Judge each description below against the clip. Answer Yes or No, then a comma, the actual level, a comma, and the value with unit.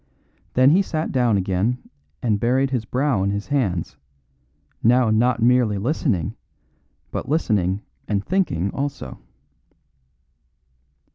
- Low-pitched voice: Yes, low, 120 Hz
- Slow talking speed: Yes, slow, 115 wpm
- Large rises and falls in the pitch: No, average, 4.9 semitones